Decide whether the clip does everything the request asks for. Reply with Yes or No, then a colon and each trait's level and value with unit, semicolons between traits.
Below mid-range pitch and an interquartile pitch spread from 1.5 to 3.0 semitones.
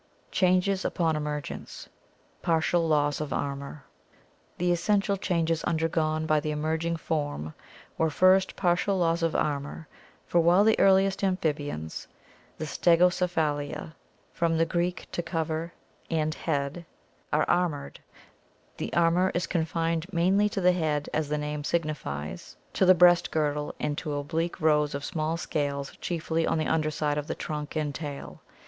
No: medium, 160 Hz; average, 2.7 semitones